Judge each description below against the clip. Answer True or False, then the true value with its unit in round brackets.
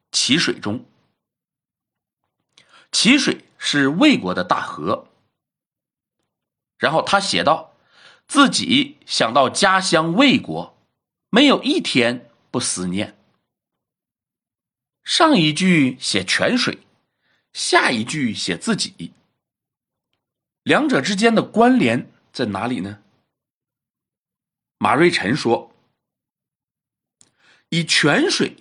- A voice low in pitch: False (190 Hz)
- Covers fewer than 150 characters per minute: True (130 characters per minute)